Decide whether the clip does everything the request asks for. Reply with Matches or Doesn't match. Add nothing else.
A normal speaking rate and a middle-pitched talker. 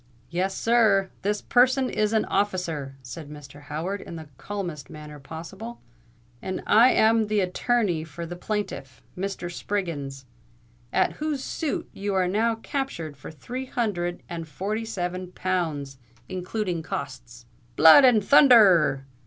Doesn't match